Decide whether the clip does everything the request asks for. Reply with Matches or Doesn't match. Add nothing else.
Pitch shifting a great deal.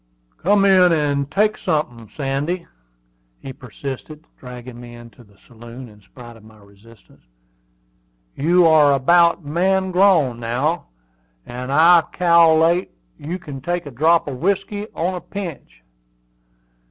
Matches